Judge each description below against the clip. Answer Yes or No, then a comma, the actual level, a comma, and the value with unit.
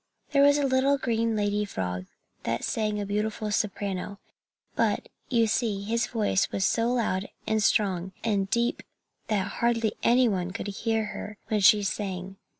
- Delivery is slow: No, average, 160 wpm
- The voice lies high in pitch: Yes, high, 210 Hz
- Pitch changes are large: No, average, 2.7 semitones